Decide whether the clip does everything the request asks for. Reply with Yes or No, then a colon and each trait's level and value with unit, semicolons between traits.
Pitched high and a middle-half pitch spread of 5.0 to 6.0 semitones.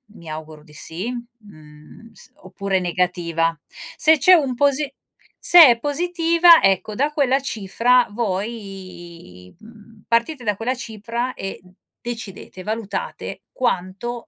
Yes: high, 225 Hz; wide, 5.4 semitones